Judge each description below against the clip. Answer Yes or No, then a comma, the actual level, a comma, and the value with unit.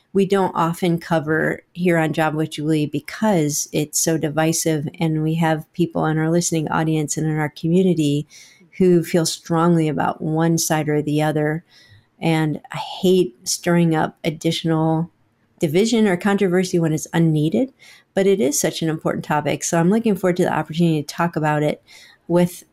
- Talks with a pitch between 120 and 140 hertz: No, medium, 165 Hz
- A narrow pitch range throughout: Yes, narrow, 2.2 semitones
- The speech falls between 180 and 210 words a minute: No, average, 170 wpm